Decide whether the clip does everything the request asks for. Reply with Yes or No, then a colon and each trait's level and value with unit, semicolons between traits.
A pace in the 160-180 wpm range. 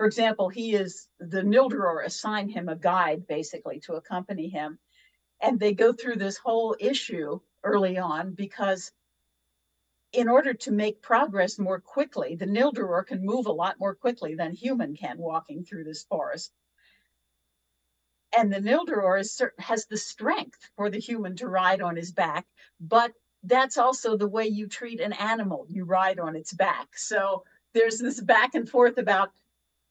Yes: average, 165 wpm